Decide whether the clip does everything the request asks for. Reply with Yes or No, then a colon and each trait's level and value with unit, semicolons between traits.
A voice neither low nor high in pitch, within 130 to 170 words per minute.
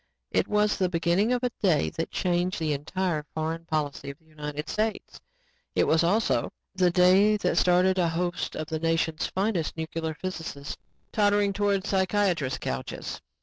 Yes: medium, 175 Hz; average, 160 wpm